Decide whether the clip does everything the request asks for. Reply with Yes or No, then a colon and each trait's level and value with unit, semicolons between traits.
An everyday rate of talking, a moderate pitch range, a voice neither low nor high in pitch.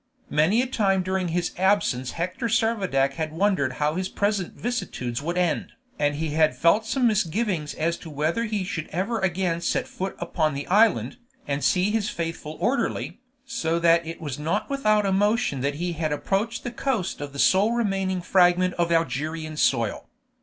Yes: average, 175 wpm; average, 4.8 semitones; medium, 175 Hz